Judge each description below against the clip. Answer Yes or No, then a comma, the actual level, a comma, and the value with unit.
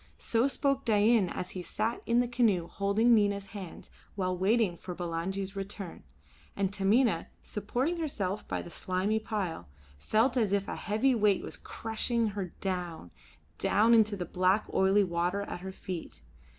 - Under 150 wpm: No, average, 160 wpm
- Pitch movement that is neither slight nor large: Yes, average, 3.4 semitones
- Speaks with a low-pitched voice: No, high, 200 Hz